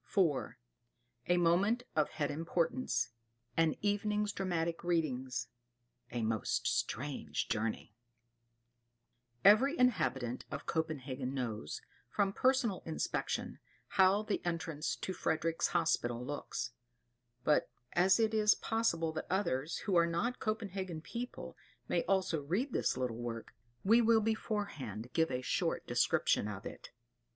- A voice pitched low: No, medium, 170 Hz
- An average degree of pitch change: No, wide, 7.1 semitones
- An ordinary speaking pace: No, slow, 125 wpm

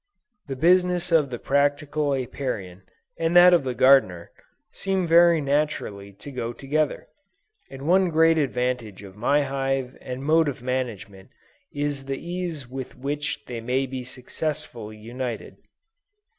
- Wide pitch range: No, average, 3.8 semitones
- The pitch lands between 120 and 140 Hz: Yes, low, 135 Hz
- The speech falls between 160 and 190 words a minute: No, average, 140 wpm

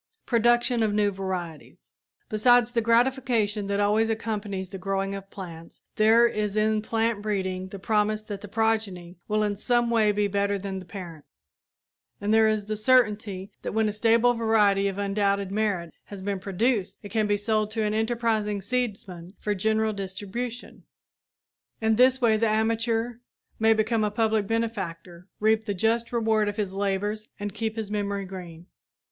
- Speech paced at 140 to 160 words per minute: No, average, 170 wpm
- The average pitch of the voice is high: Yes, high, 210 Hz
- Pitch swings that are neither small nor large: No, narrow, 2.1 semitones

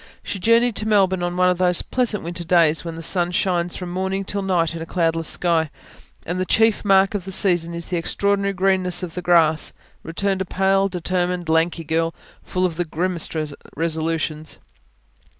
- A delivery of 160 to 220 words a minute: Yes, average, 185 wpm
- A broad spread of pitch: No, narrow, 2.5 semitones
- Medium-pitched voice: Yes, medium, 180 Hz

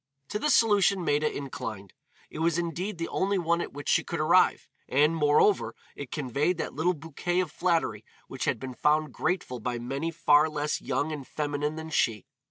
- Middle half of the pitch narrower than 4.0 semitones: Yes, average, 3.3 semitones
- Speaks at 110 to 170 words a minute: No, average, 185 wpm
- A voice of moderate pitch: Yes, medium, 155 Hz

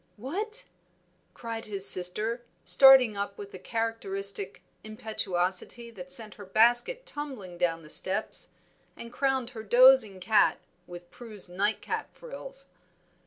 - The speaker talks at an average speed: No, slow, 120 wpm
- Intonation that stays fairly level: No, average, 4.5 semitones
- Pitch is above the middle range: Yes, high, 220 Hz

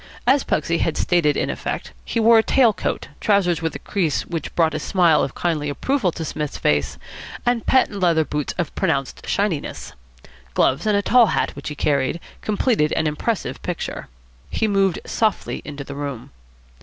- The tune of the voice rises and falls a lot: Yes, wide, 5.7 semitones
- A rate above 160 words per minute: Yes, average, 180 wpm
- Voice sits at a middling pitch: Yes, medium, 170 Hz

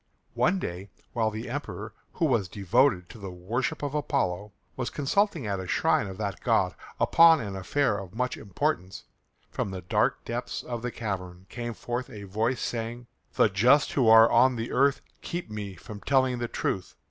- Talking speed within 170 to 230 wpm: Yes, average, 180 wpm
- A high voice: No, low, 115 Hz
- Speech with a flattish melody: No, average, 4.6 semitones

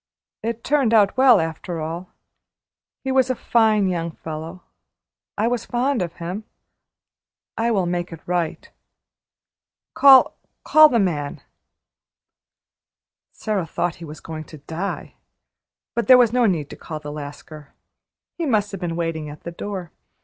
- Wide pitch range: Yes, wide, 6.1 semitones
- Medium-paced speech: Yes, average, 150 wpm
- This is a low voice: No, medium, 180 Hz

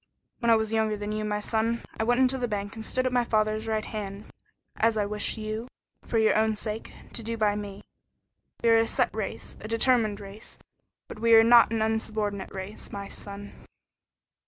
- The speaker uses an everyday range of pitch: No, narrow, 1.6 semitones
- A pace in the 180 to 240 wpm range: Yes, fast, 205 wpm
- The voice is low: No, high, 220 Hz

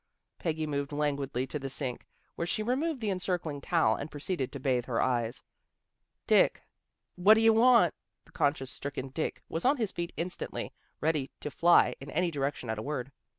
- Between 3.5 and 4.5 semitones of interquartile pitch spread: No, average, 5.1 semitones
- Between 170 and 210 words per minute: Yes, average, 195 wpm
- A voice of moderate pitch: Yes, medium, 150 Hz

